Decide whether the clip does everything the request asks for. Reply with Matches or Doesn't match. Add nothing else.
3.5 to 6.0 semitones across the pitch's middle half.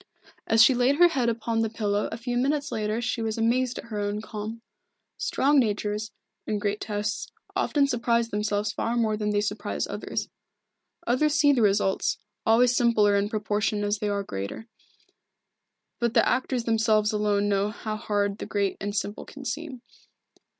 Doesn't match